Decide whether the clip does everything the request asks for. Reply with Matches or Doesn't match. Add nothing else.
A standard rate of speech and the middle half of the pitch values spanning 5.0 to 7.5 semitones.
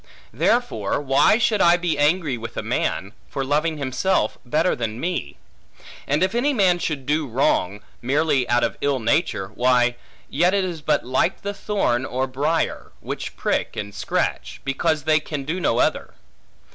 Matches